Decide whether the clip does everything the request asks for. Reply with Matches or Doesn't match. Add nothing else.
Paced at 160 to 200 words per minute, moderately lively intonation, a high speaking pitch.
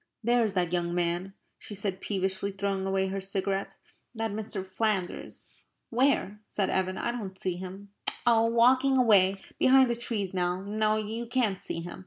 Matches